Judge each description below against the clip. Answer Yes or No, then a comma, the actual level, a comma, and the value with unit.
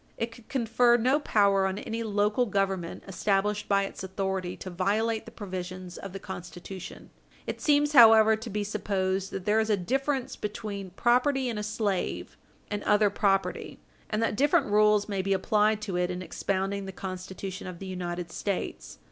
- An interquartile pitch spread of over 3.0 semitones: No, narrow, 2.6 semitones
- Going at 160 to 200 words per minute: Yes, average, 175 wpm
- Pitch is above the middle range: Yes, high, 200 Hz